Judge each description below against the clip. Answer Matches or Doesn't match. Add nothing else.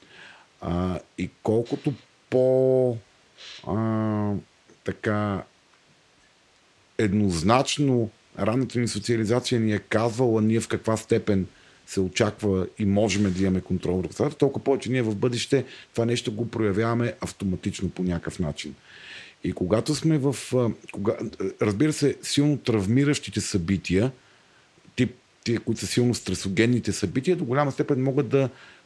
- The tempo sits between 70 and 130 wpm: Matches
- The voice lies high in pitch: Doesn't match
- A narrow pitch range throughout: Doesn't match